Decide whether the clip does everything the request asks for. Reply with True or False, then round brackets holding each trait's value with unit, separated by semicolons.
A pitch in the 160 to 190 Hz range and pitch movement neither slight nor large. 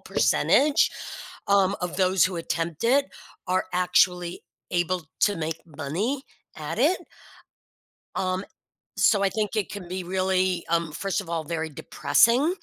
True (185 Hz; 3.0 semitones)